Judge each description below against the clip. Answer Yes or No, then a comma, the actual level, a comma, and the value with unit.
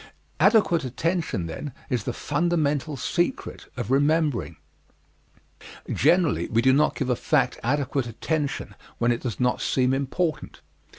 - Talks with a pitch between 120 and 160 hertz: Yes, medium, 140 Hz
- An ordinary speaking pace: No, slow, 130 wpm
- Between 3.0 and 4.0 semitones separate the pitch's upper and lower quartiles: No, average, 4.5 semitones